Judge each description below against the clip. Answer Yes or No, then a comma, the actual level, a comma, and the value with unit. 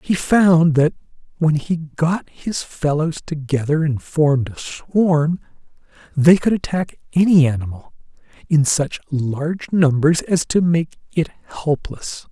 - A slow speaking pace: Yes, slow, 130 wpm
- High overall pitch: No, medium, 155 Hz